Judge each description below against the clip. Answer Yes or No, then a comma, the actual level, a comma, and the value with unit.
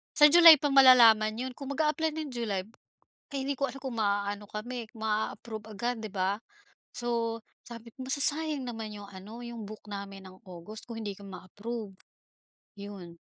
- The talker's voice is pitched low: No, high, 225 Hz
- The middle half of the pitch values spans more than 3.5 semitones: Yes, average, 4.2 semitones